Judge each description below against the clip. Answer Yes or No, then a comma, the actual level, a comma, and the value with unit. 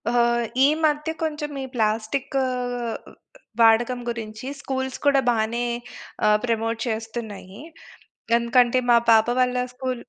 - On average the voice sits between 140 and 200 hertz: No, high, 235 Hz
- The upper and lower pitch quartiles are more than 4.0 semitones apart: No, narrow, 2.6 semitones